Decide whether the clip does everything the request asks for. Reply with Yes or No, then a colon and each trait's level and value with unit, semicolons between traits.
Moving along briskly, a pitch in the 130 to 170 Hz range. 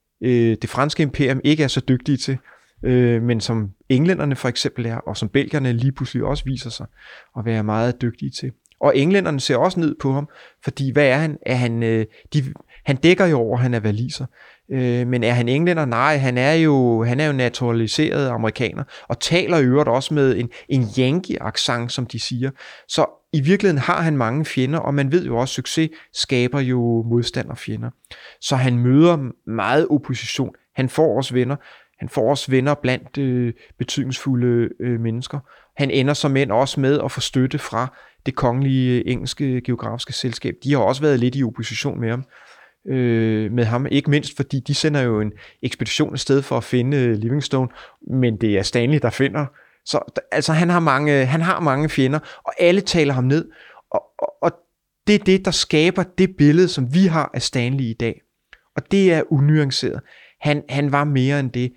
No: average, 195 wpm; low, 135 Hz